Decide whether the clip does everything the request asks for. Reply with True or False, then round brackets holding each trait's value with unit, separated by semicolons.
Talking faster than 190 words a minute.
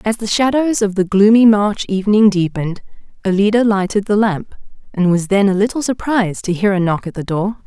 True (205 wpm)